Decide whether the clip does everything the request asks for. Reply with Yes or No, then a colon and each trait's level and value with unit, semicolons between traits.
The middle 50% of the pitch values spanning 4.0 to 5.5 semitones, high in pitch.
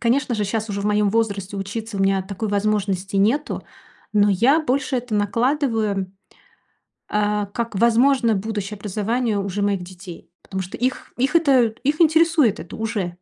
No: average, 3.5 semitones; high, 210 Hz